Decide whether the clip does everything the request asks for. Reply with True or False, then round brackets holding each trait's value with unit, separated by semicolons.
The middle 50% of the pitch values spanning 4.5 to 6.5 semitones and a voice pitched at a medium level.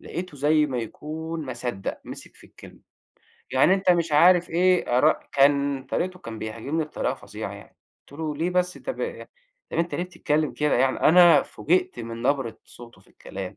True (5.2 semitones; 150 Hz)